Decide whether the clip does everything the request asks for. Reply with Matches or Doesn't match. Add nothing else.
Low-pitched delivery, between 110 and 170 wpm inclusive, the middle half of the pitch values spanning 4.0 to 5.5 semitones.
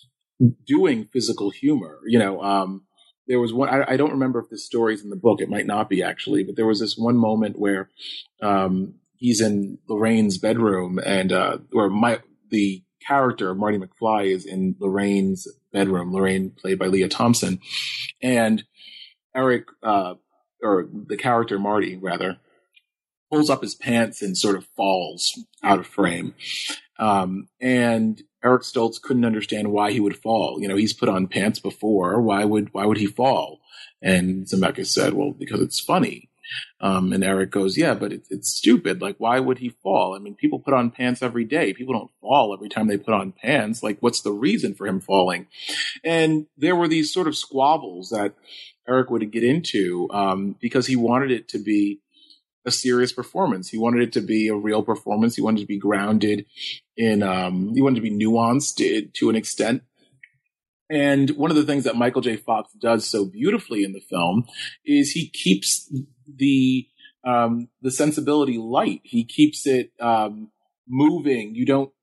Doesn't match